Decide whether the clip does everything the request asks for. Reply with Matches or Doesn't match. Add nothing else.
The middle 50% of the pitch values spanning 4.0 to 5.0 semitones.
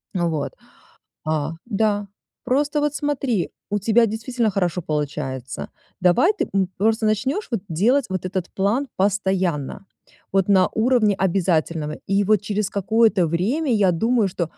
Matches